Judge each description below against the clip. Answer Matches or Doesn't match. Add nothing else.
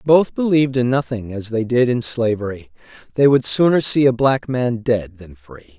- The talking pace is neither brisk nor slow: Matches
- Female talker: Doesn't match